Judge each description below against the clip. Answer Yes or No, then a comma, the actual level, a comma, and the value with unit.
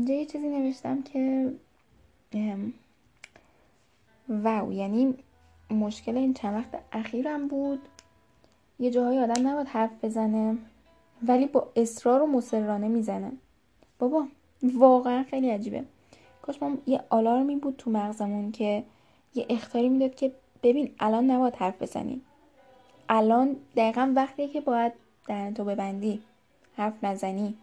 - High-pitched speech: Yes, high, 245 Hz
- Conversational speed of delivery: Yes, average, 120 wpm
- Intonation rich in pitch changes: No, average, 3.4 semitones